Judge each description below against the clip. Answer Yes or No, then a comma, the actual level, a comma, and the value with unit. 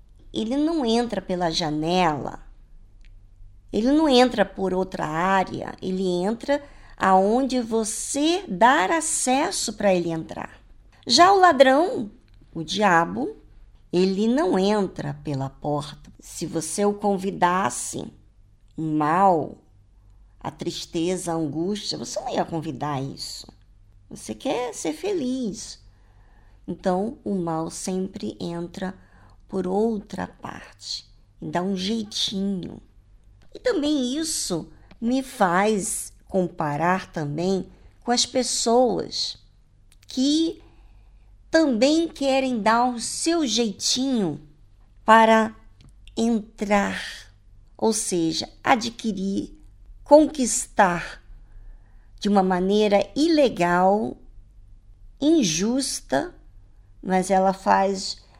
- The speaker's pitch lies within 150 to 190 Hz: Yes, medium, 185 Hz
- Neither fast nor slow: No, slow, 95 wpm